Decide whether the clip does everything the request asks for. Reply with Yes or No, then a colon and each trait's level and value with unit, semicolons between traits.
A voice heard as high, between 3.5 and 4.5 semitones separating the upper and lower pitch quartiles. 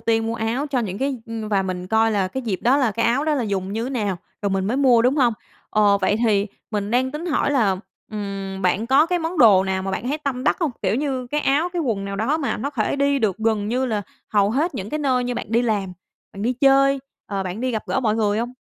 No: high, 230 Hz; average, 5.0 semitones